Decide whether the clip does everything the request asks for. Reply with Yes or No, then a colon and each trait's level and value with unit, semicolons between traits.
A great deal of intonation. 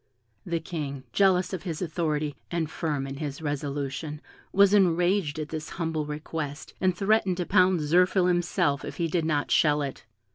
No: average, 3.4 semitones